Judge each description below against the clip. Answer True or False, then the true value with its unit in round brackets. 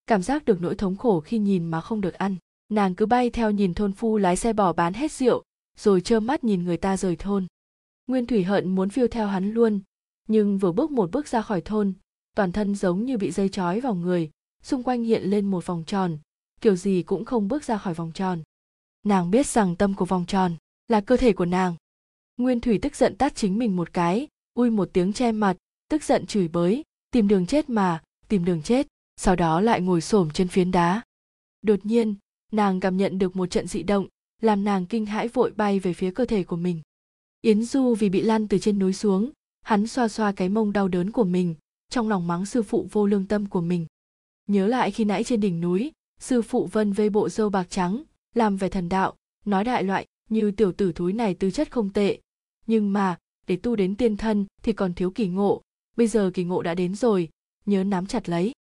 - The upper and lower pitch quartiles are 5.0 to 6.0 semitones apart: False (3.4 semitones)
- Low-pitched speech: False (205 Hz)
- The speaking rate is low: False (230 wpm)